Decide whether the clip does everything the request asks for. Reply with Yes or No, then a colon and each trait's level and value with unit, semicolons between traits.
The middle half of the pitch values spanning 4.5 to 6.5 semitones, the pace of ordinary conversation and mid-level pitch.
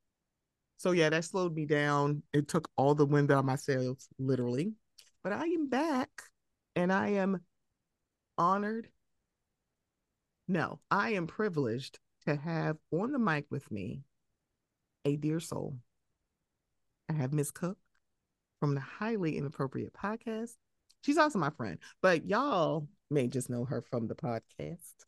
Yes: wide, 5.6 semitones; average, 145 wpm; medium, 155 Hz